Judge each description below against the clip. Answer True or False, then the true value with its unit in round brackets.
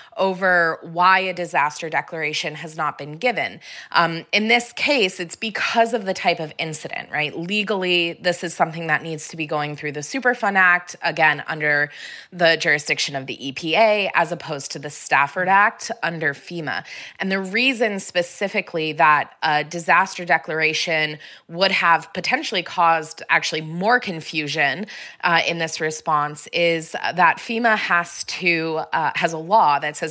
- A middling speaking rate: True (155 wpm)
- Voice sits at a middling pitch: True (170 Hz)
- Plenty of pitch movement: False (3.4 semitones)